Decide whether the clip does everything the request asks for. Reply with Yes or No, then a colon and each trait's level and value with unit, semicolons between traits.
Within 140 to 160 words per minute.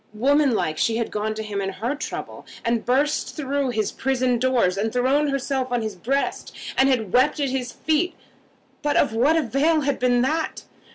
No: average, 185 wpm